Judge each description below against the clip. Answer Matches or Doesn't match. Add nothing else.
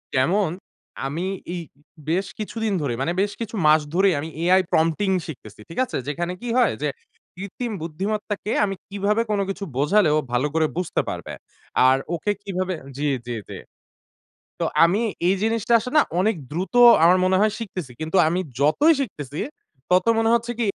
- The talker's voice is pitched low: Doesn't match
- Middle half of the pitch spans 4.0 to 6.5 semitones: Matches